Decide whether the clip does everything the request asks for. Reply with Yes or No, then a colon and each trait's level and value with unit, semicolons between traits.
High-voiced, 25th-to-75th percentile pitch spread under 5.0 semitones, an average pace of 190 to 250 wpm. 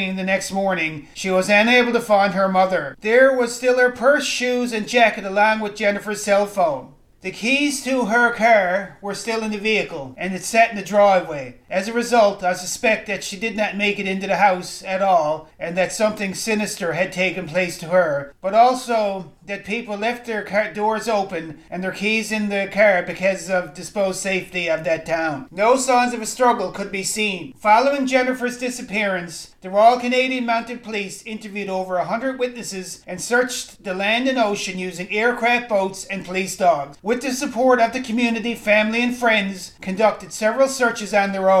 Yes: high, 205 Hz; average, 3.8 semitones; average, 195 wpm